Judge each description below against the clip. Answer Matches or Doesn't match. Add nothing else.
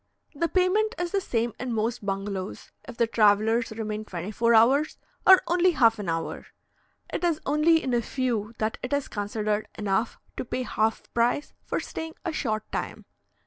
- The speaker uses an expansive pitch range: Matches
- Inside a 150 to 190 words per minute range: Matches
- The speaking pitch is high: Matches